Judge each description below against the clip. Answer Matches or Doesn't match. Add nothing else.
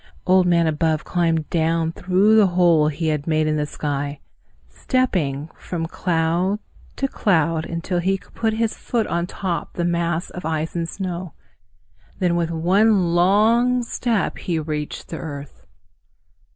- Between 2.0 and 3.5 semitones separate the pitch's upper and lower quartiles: Matches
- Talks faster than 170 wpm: Doesn't match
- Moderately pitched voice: Matches